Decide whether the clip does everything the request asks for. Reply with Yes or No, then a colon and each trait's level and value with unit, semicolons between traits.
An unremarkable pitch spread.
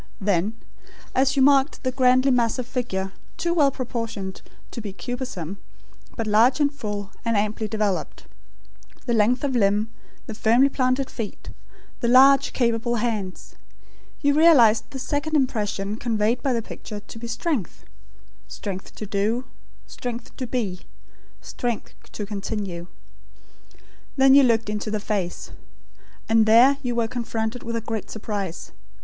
Yes: average, 3.5 semitones